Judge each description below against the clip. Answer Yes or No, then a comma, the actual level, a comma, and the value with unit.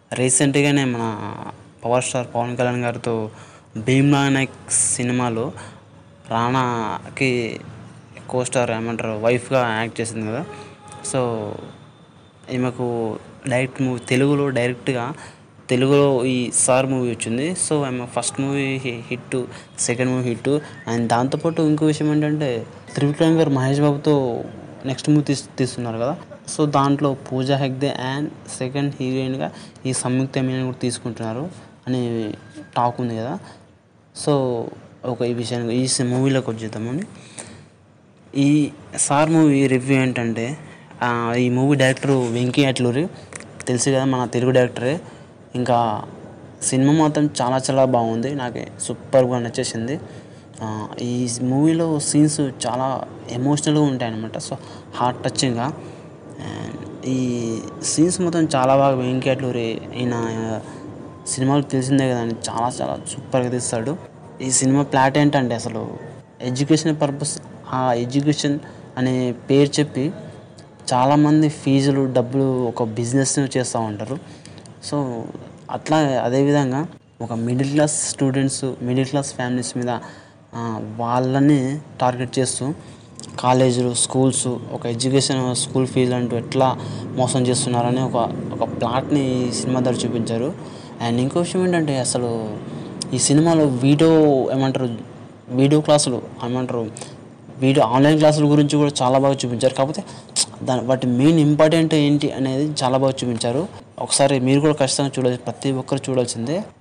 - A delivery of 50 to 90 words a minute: No, average, 120 wpm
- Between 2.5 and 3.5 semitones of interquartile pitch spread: Yes, average, 2.8 semitones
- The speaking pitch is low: Yes, low, 130 Hz